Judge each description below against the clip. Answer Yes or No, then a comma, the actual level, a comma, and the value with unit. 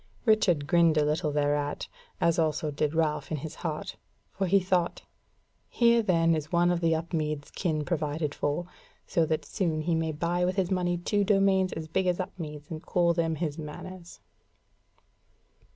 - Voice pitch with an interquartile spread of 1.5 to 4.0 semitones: Yes, average, 2.7 semitones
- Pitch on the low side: No, medium, 165 Hz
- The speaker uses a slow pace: No, average, 170 wpm